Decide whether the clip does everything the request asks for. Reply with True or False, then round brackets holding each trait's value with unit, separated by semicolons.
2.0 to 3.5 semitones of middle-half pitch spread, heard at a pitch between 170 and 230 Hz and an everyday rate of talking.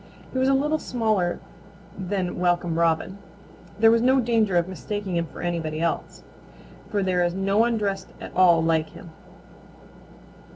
False (4.3 semitones; 190 Hz; 160 wpm)